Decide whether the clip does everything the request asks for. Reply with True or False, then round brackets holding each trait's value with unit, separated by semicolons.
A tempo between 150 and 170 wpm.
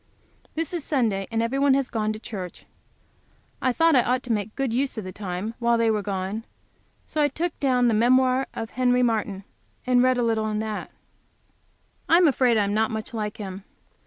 False (205 wpm)